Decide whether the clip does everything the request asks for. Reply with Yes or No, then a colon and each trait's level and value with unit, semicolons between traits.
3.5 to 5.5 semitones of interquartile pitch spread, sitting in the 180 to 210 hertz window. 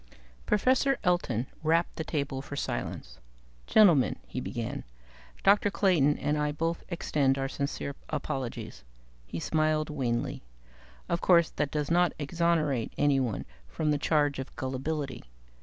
No: average, 3.8 semitones; medium, 150 Hz